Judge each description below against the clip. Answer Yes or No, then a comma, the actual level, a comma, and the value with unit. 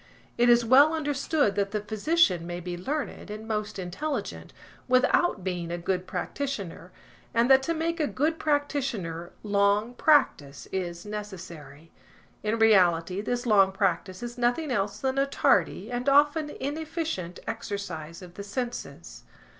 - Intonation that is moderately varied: No, wide, 7.0 semitones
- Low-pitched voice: No, high, 215 Hz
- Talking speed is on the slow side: No, average, 145 wpm